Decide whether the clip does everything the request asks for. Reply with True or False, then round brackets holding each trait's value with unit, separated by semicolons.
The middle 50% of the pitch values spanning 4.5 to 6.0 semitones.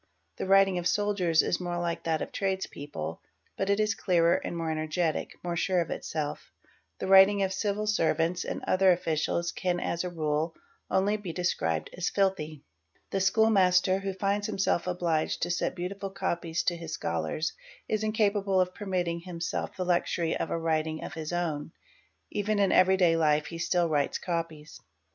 False (2.9 semitones)